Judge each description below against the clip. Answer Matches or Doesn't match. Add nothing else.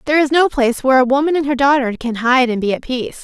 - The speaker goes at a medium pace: Doesn't match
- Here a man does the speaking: Doesn't match